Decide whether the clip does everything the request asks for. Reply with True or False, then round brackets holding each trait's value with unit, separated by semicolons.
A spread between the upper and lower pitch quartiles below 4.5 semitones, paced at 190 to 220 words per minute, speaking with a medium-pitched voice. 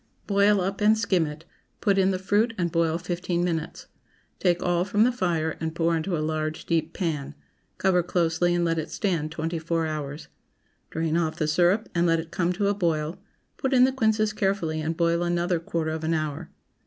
True (2.9 semitones; 205 wpm; 170 Hz)